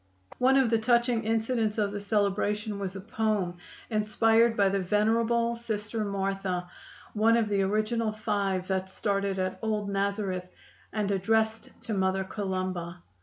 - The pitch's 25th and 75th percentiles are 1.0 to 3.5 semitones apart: Yes, narrow, 2.4 semitones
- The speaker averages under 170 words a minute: Yes, average, 145 wpm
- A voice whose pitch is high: Yes, high, 210 Hz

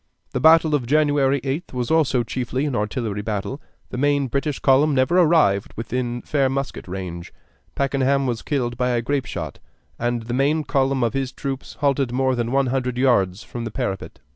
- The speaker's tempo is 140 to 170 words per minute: No, average, 185 wpm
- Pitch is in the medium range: No, low, 130 Hz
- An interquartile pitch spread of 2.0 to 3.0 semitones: Yes, average, 2.7 semitones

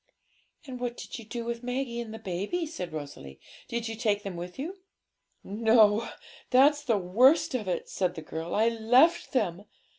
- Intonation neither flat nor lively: Yes, average, 4.7 semitones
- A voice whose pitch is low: No, high, 225 Hz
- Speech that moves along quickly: No, average, 175 wpm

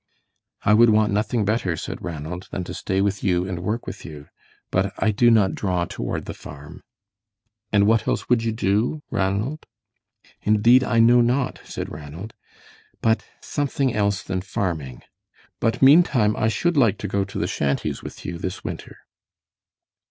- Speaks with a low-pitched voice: Yes, low, 105 Hz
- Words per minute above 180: No, average, 165 wpm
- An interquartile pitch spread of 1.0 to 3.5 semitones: No, average, 3.9 semitones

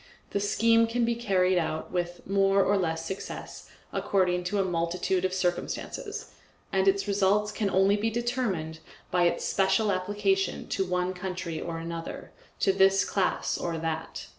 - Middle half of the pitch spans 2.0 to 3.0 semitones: Yes, narrow, 2.4 semitones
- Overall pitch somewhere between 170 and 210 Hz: Yes, high, 190 Hz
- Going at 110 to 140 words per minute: No, average, 160 wpm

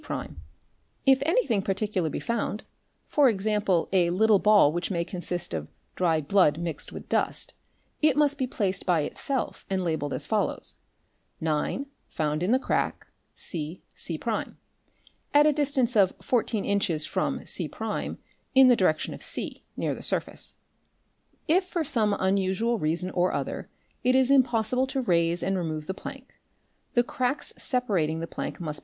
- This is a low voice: No, high, 200 Hz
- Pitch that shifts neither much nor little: No, wide, 6.8 semitones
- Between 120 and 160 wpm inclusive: Yes, average, 155 wpm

